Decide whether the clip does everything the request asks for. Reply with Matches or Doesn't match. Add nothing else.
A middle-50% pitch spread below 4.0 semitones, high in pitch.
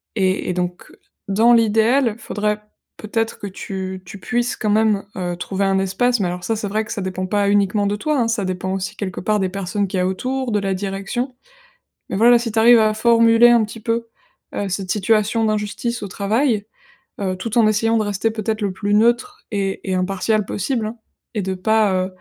Matches